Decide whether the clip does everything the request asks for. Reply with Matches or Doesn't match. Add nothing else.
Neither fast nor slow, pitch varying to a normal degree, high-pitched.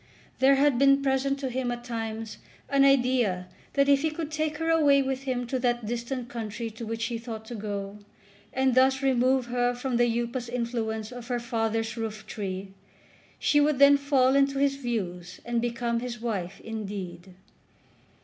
Matches